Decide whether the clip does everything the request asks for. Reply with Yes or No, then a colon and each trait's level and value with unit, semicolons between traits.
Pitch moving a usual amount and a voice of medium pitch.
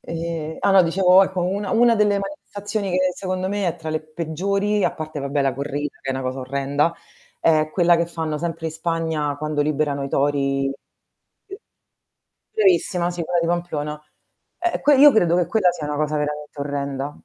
Yes: average, 3.9 semitones; medium, 165 Hz